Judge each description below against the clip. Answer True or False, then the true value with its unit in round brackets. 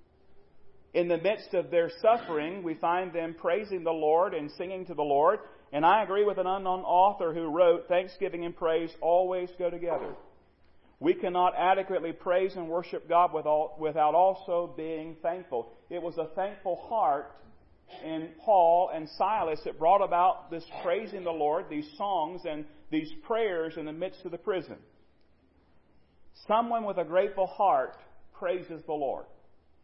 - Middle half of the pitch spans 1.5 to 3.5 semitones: True (2.9 semitones)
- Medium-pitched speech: True (170 Hz)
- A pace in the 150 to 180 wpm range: True (155 wpm)